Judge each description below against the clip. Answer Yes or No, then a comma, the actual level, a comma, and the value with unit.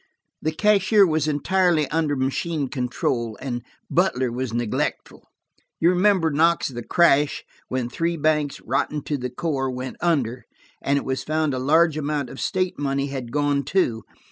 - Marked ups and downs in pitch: No, average, 4.0 semitones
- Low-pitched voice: No, medium, 145 Hz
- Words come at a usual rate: Yes, average, 160 wpm